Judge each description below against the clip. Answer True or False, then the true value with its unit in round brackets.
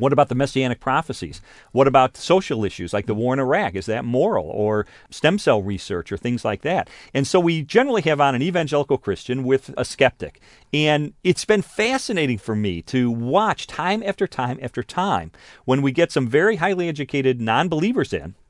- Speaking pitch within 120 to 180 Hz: True (135 Hz)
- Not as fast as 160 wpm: False (195 wpm)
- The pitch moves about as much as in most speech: False (6.4 semitones)